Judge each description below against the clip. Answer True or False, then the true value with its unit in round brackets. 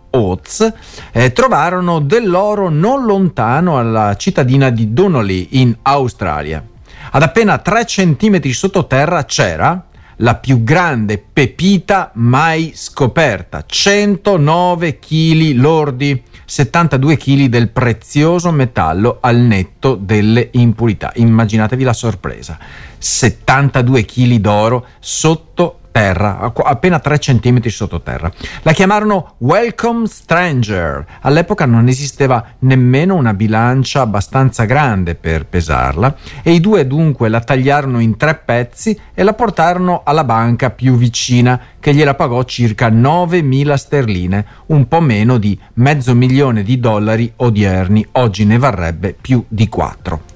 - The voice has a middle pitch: False (130 Hz)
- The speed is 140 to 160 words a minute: False (115 wpm)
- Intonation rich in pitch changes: True (6.1 semitones)